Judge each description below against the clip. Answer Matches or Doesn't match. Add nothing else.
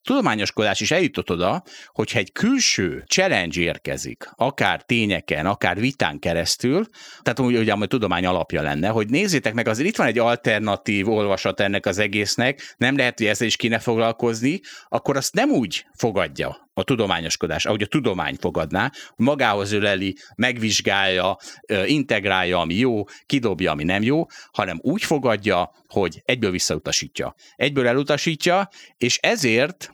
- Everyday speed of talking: Matches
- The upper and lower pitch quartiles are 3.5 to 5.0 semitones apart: Matches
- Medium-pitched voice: Doesn't match